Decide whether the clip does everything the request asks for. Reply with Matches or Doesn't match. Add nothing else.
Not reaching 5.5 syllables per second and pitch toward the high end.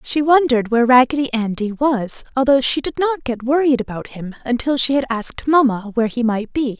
Doesn't match